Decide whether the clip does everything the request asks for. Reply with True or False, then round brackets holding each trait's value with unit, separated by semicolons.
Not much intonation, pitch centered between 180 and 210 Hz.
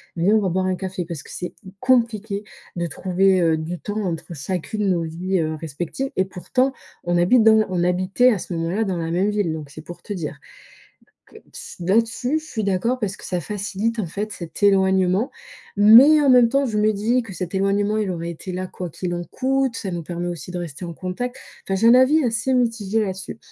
False (4.2 semitones; 190 Hz)